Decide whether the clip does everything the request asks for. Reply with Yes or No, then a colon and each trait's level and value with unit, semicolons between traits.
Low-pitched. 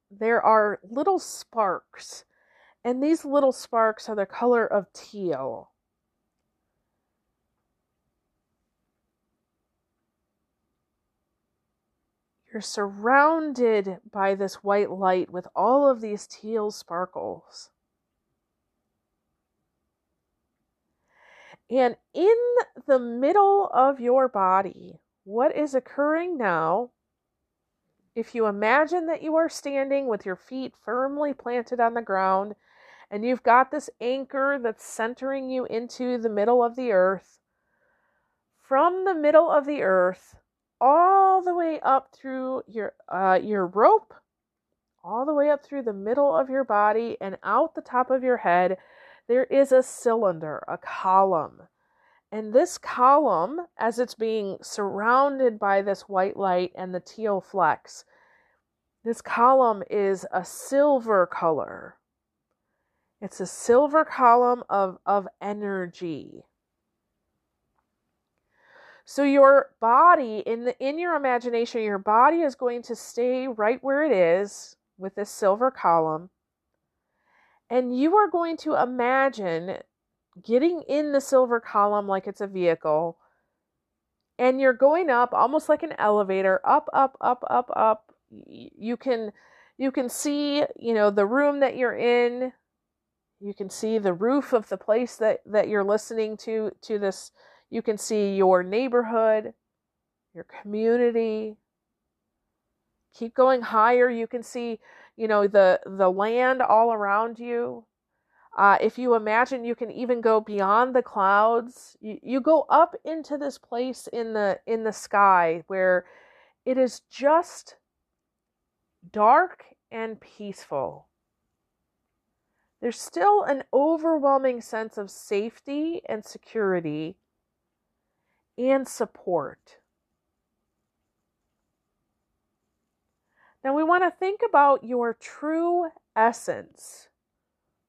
No: high, 235 Hz